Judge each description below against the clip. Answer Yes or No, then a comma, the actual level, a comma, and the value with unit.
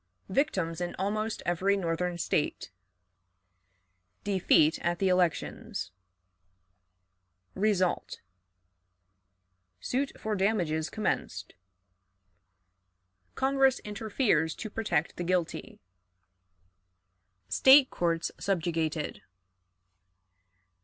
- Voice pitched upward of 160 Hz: Yes, medium, 185 Hz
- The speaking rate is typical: No, slow, 70 wpm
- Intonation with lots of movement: No, average, 4.5 semitones